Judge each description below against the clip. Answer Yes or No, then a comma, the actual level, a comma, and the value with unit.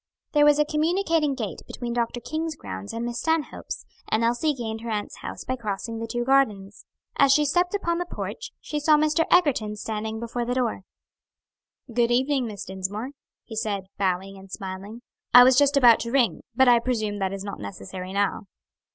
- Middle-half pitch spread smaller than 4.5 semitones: No, wide, 5.6 semitones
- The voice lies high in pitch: Yes, high, 235 Hz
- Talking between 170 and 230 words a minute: Yes, average, 190 wpm